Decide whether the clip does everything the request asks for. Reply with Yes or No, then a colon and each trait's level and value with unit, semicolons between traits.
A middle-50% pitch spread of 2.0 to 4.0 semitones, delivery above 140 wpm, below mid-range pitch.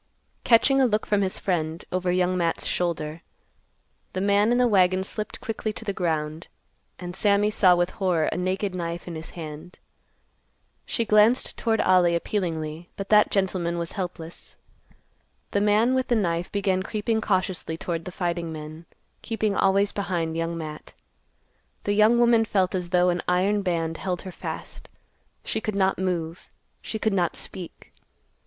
No: average, 3.4 semitones; average, 165 wpm; medium, 185 Hz